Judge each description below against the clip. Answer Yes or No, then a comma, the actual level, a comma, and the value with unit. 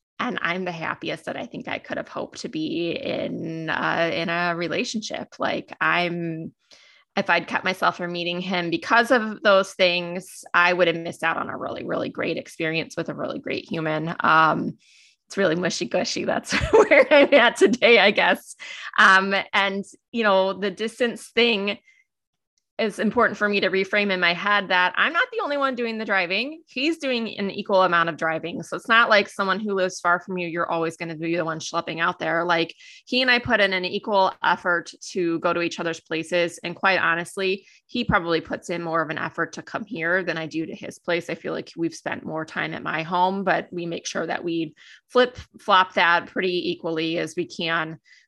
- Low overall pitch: No, medium, 185 Hz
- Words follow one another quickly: Yes, fast, 210 wpm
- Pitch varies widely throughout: No, average, 3.8 semitones